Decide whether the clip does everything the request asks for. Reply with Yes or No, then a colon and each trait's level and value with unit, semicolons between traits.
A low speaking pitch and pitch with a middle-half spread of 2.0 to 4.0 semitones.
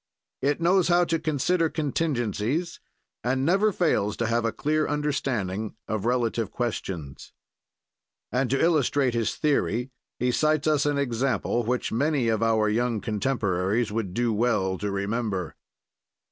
No: low, 120 Hz; average, 5.3 semitones